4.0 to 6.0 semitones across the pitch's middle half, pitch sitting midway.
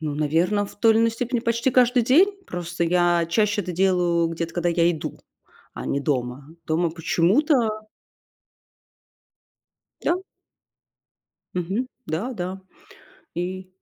Yes: average, 5.2 semitones; medium, 180 Hz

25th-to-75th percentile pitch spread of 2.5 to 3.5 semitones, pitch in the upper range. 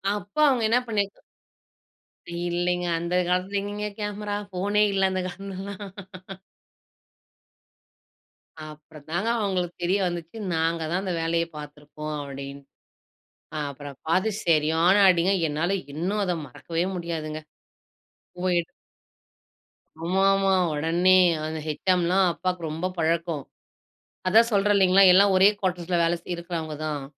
No: average, 3.2 semitones; medium, 175 Hz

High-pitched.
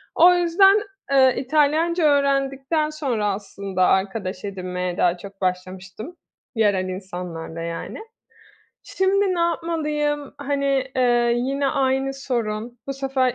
Yes: very high, 260 Hz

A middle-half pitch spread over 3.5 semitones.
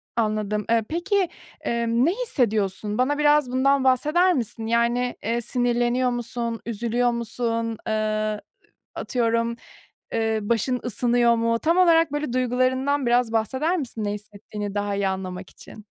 No: average, 2.8 semitones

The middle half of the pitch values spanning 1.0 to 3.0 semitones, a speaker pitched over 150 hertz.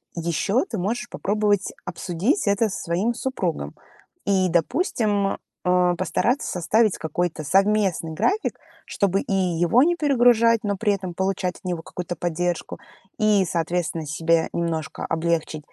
No: average, 4.1 semitones; medium, 185 Hz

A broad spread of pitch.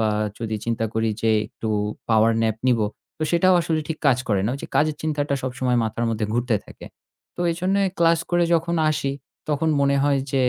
Yes: wide, 6.0 semitones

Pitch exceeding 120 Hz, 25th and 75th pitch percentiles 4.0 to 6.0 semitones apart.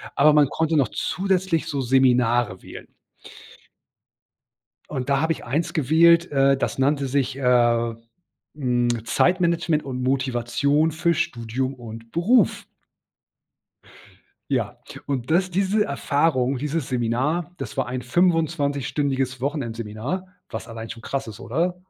Yes: low, 135 Hz; average, 4.9 semitones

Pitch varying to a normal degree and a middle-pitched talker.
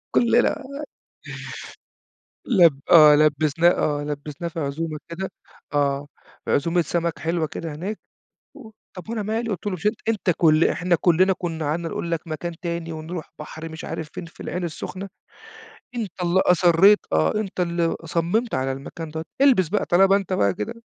Yes: average, 3.3 semitones; medium, 170 Hz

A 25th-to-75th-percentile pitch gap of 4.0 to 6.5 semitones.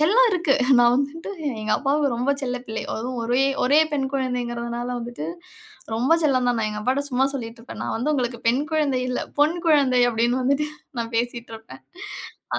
No: average, 2.9 semitones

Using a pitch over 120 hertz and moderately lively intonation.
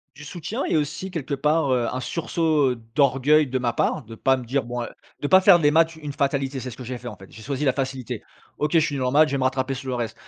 Yes: low, 135 Hz; average, 3.0 semitones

